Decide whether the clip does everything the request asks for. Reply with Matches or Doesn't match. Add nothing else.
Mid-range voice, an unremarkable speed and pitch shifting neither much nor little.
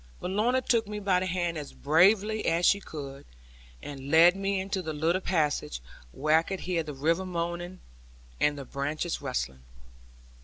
Matches